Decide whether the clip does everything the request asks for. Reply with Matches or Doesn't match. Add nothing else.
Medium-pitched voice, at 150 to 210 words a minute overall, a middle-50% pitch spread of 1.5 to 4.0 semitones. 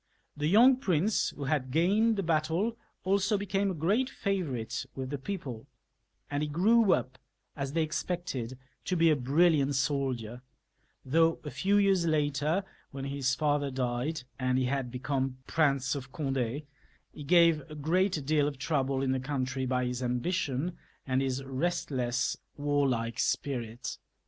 Doesn't match